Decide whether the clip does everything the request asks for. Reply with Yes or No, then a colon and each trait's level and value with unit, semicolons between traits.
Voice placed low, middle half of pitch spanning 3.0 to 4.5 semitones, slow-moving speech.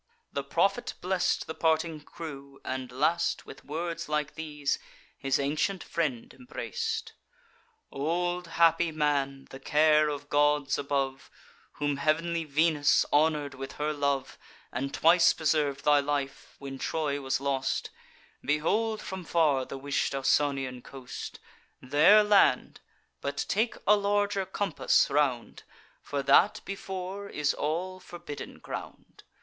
No: medium, 150 Hz; average, 3.5 semitones; slow, 125 wpm